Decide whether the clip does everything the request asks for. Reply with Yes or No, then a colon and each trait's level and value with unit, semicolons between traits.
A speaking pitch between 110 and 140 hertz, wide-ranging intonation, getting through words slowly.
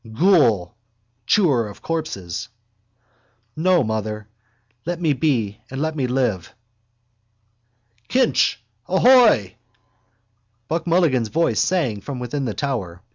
Yes: low, 135 Hz; wide, 7.4 semitones; slow, 110 wpm